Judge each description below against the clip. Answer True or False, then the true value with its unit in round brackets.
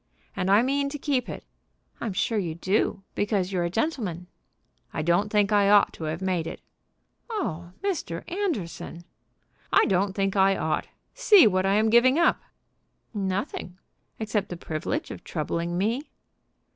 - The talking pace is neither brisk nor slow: True (160 wpm)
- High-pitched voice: True (200 Hz)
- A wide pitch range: False (5.0 semitones)